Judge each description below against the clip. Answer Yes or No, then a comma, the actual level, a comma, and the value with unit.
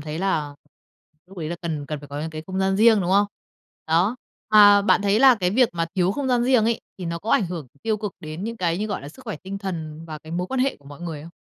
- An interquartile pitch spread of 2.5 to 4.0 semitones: No, average, 4.8 semitones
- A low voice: No, medium, 185 Hz